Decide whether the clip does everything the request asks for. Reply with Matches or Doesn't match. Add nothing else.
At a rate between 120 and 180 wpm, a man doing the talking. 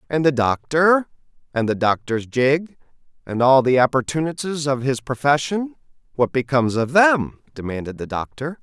Matches